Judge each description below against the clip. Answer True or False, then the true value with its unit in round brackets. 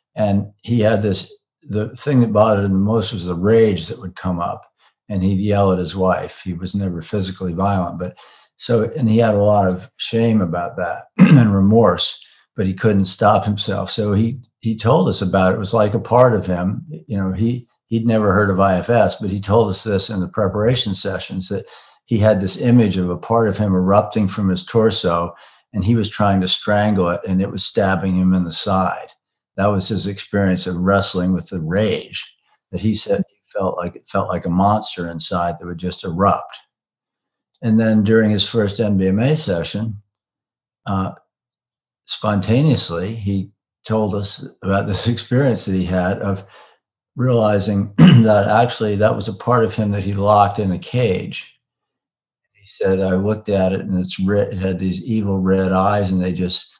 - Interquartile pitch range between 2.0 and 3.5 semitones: True (2.8 semitones)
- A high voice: False (100 Hz)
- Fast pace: False (195 wpm)